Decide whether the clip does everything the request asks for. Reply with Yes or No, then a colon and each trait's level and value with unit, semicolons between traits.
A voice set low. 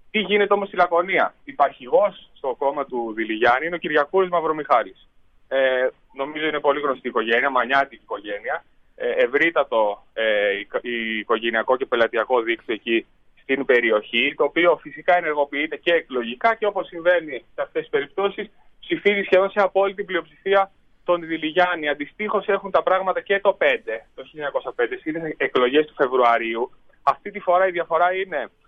No: medium, 170 Hz